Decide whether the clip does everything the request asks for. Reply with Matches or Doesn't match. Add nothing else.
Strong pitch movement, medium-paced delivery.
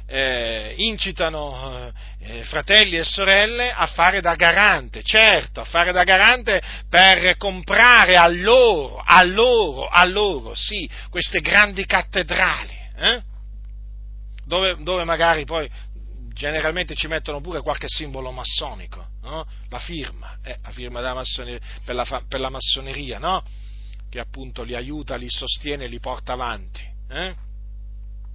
Matches